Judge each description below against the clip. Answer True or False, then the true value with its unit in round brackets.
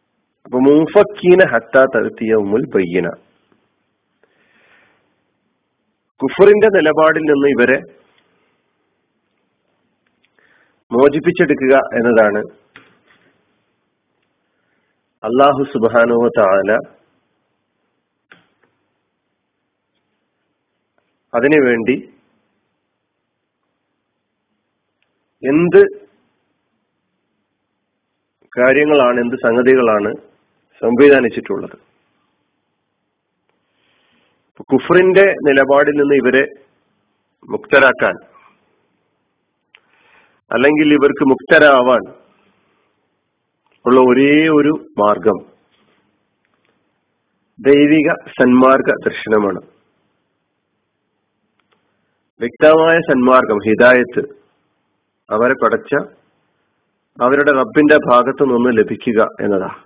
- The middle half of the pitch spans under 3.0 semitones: False (3.4 semitones)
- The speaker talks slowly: True (45 wpm)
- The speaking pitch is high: False (140 Hz)